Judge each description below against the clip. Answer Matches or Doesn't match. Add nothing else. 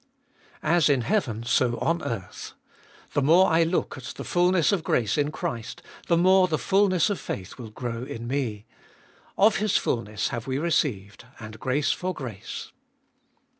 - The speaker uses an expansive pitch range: Matches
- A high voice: Doesn't match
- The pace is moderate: Matches